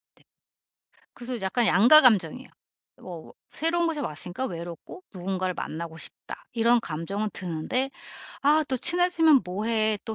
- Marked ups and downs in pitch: Yes, wide, 7.1 semitones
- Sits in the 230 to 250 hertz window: No, high, 220 Hz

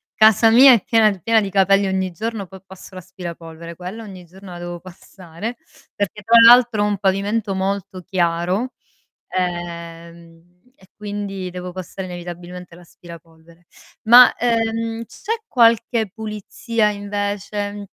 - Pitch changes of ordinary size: Yes, average, 3.7 semitones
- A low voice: No, high, 195 Hz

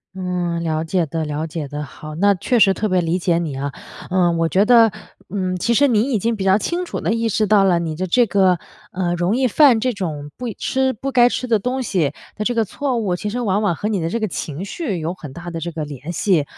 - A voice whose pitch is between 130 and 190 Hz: Yes, medium, 185 Hz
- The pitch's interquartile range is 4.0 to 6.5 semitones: Yes, average, 5.3 semitones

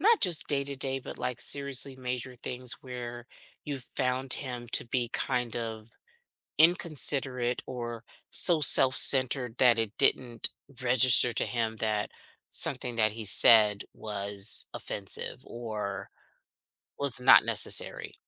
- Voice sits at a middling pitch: No, low, 125 Hz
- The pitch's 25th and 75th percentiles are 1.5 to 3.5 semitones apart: Yes, average, 2.8 semitones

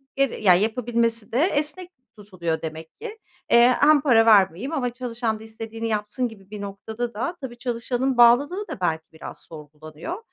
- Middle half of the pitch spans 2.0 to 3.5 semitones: No, average, 4.1 semitones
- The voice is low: No, high, 230 Hz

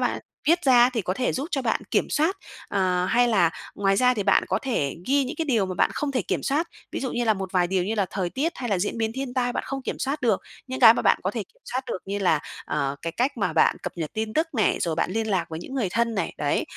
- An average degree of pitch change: No, wide, 5.8 semitones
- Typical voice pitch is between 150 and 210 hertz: No, high, 225 Hz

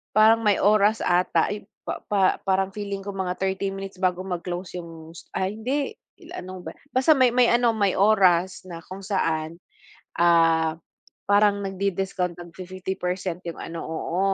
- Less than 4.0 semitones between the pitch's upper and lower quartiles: Yes, narrow, 2.6 semitones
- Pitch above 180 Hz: Yes, high, 190 Hz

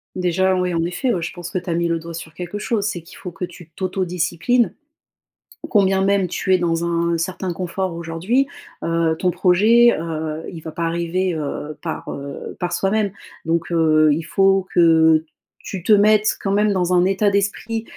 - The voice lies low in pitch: No, medium, 175 Hz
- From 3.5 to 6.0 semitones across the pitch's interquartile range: No, average, 2.7 semitones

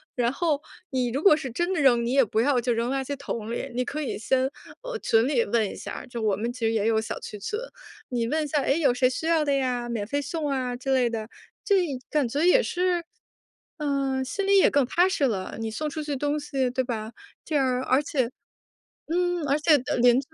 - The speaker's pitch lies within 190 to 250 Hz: No, very high, 265 Hz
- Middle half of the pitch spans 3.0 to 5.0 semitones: Yes, average, 3.9 semitones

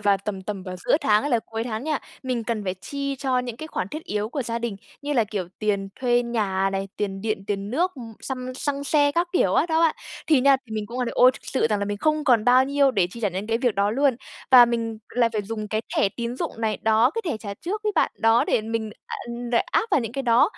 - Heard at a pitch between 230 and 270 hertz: Yes, high, 235 Hz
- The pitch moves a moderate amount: Yes, average, 4.2 semitones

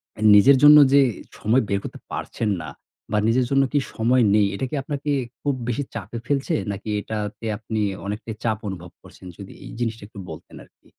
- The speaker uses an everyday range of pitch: Yes, average, 4.4 semitones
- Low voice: Yes, low, 115 Hz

